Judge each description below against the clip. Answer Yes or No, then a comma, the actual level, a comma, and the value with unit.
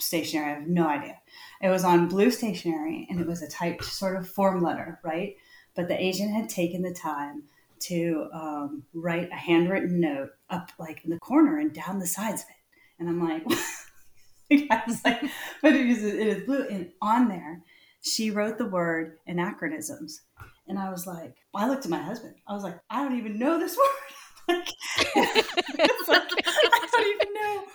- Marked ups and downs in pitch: Yes, wide, 8.5 semitones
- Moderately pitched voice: No, high, 195 Hz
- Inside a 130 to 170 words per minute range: No, average, 190 wpm